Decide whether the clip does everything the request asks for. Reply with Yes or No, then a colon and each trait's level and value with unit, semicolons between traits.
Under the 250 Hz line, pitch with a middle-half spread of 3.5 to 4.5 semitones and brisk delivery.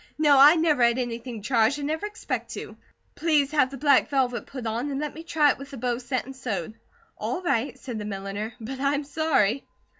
No: very high, 270 Hz; average, 3.8 semitones; fast, 215 wpm